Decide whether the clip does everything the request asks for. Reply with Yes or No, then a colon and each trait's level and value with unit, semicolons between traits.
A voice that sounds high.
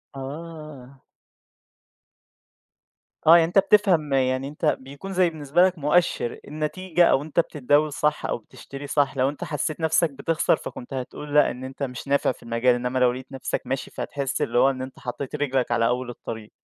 No: medium, 140 Hz